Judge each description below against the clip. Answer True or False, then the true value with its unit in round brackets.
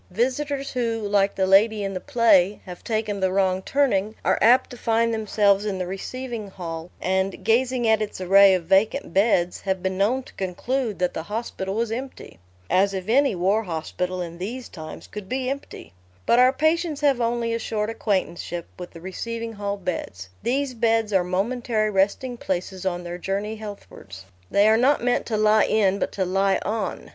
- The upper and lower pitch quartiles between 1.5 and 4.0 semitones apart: True (3.7 semitones)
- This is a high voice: True (205 Hz)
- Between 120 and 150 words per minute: False (190 wpm)